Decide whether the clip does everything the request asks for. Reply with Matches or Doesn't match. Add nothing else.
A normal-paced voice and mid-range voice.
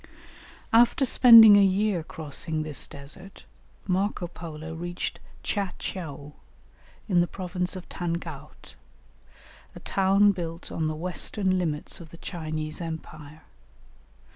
Doesn't match